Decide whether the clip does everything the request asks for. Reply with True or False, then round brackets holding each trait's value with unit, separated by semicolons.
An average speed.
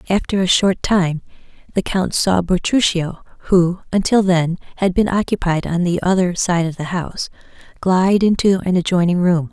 True (165 wpm)